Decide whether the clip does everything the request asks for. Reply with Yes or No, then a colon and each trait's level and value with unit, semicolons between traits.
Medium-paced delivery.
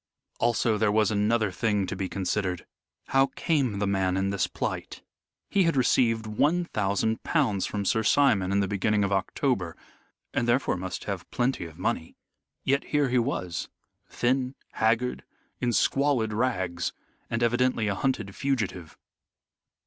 Yes: average, 150 wpm